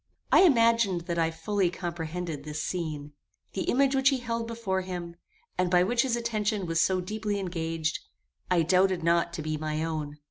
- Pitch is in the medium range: Yes, medium, 180 Hz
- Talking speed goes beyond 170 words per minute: Yes, average, 180 wpm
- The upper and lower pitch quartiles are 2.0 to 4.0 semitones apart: No, average, 4.7 semitones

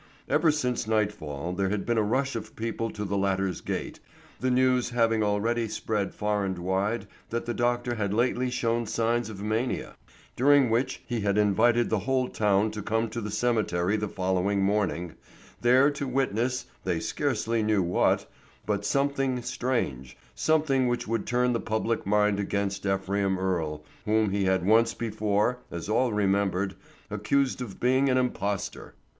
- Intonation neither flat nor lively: Yes, average, 3.5 semitones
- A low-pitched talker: Yes, low, 110 Hz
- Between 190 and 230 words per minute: No, average, 165 wpm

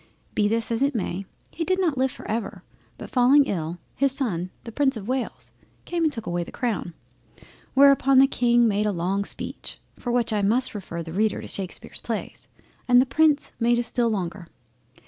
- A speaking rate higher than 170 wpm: Yes, average, 200 wpm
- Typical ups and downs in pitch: Yes, average, 4.9 semitones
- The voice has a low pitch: No, high, 235 Hz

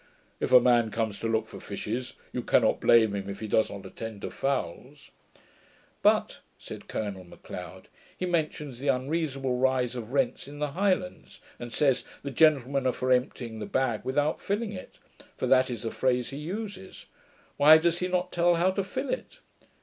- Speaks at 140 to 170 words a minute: No, average, 185 wpm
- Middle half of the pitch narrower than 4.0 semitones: No, average, 5.3 semitones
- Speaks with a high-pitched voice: No, low, 130 Hz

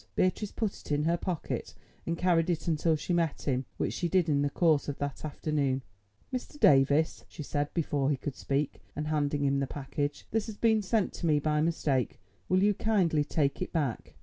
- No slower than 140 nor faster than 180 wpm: No, fast, 205 wpm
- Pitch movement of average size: Yes, average, 3.6 semitones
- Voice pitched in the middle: Yes, medium, 155 Hz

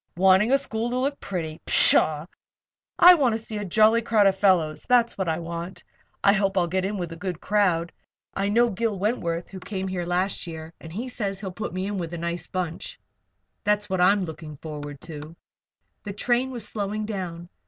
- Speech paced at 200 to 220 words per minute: Yes, fast, 205 wpm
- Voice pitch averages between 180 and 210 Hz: Yes, high, 190 Hz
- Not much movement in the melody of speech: No, average, 3.9 semitones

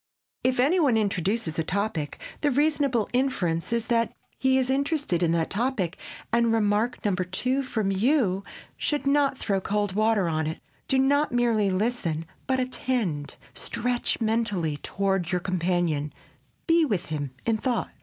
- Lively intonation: Yes, wide, 6.1 semitones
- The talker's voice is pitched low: No, high, 220 Hz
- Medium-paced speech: Yes, average, 155 wpm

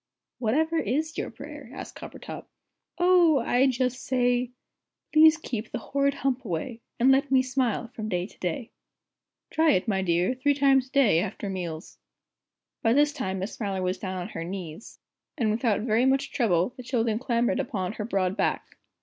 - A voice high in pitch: Yes, high, 235 Hz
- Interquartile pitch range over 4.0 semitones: Yes, wide, 5.6 semitones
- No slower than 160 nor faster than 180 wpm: Yes, average, 175 wpm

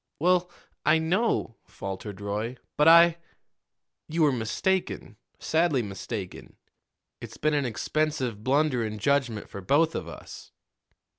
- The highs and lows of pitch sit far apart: Yes, wide, 7.1 semitones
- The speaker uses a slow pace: Yes, slow, 130 wpm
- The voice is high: No, medium, 140 Hz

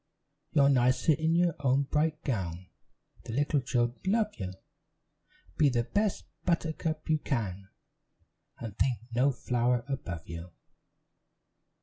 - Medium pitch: No, low, 130 Hz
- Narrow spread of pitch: No, average, 5.0 semitones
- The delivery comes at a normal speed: No, slow, 120 wpm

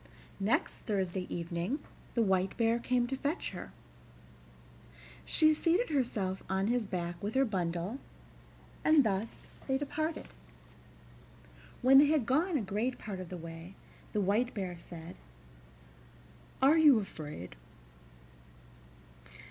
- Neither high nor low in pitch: No, high, 215 Hz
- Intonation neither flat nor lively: No, wide, 6.4 semitones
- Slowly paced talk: Yes, slow, 125 wpm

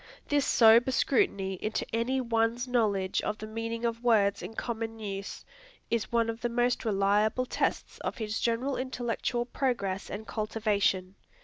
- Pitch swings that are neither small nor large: No, narrow, 2.3 semitones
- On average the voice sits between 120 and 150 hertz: No, high, 225 Hz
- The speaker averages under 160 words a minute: Yes, average, 150 wpm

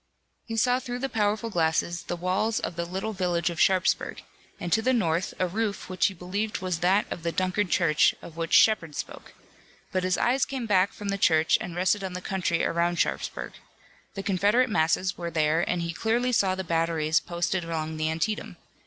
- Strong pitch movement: No, average, 3.8 semitones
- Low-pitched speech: No, medium, 185 Hz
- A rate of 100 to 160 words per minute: No, average, 200 wpm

